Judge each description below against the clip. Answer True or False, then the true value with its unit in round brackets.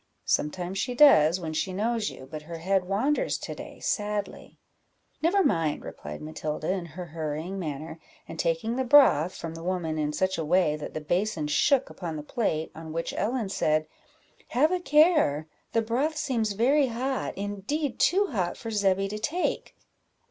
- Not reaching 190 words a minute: True (175 wpm)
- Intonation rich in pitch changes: True (7.0 semitones)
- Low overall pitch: False (190 Hz)